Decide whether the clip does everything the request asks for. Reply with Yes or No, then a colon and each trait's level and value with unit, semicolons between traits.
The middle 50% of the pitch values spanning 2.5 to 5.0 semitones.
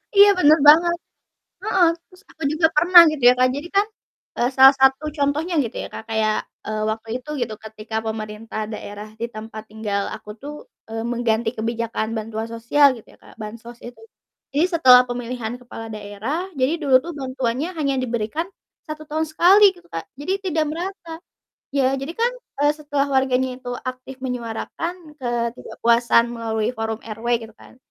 No: wide, 5.4 semitones